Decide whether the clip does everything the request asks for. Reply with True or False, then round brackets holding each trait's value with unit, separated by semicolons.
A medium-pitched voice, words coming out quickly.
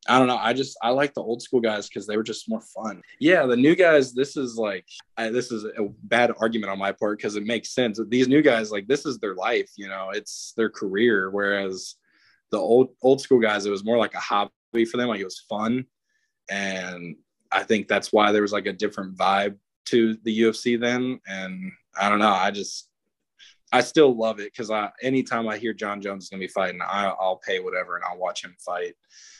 False (110 Hz; 230 wpm)